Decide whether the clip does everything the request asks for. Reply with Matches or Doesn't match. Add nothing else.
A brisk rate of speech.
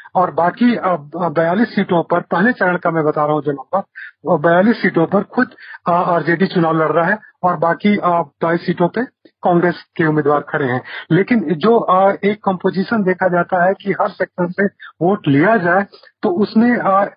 Doesn't match